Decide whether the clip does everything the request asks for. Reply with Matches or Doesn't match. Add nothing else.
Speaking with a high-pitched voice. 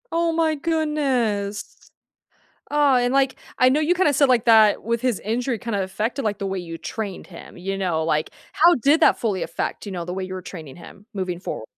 Matches